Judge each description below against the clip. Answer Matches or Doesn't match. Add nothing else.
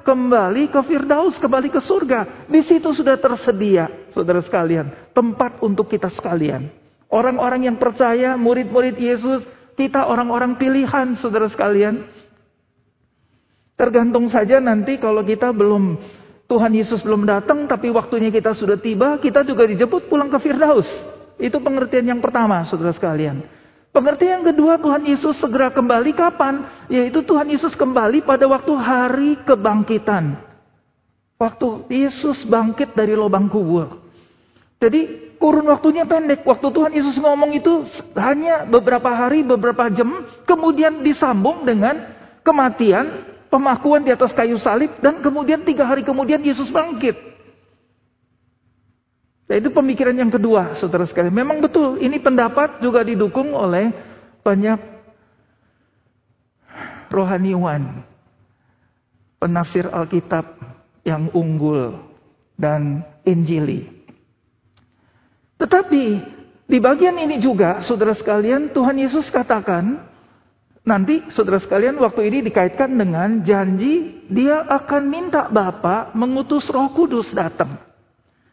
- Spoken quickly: Doesn't match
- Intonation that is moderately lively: Doesn't match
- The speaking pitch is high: Matches